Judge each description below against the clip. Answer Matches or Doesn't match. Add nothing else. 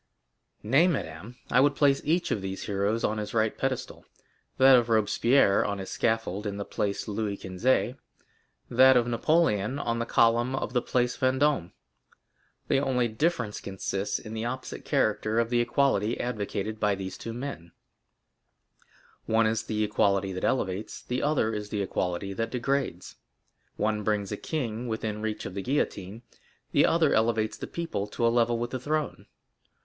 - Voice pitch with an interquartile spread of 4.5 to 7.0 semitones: Doesn't match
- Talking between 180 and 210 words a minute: Doesn't match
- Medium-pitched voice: Doesn't match